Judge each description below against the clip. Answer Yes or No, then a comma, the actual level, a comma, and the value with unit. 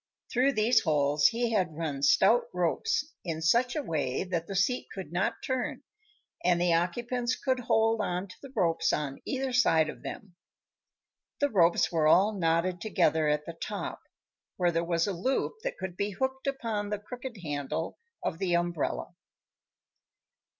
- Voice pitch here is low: No, medium, 185 Hz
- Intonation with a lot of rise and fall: Yes, wide, 6.7 semitones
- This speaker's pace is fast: No, average, 165 wpm